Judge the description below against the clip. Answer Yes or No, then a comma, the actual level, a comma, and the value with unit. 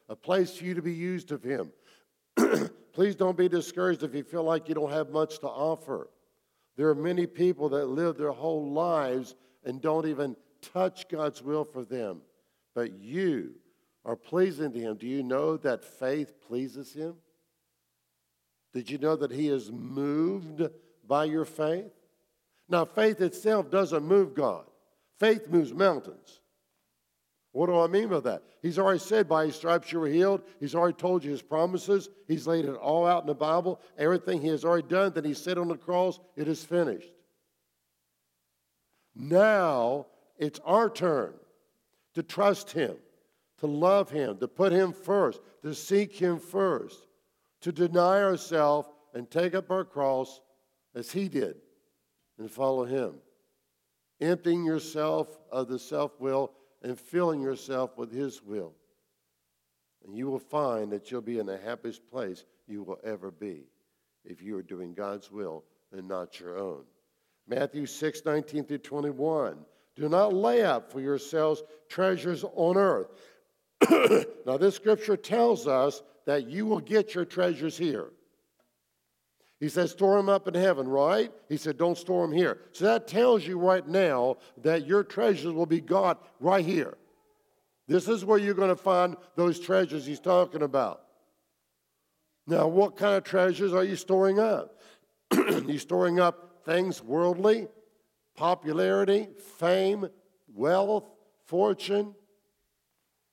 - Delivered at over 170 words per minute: No, average, 155 wpm